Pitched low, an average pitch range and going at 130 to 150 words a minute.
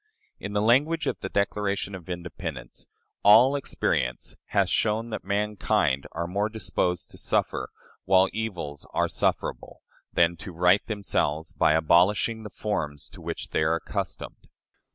Yes: very low, 95 Hz; average, 4.2 semitones; average, 145 wpm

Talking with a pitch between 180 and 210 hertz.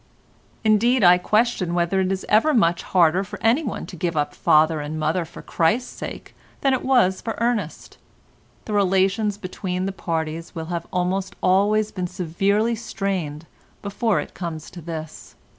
Yes: medium, 185 Hz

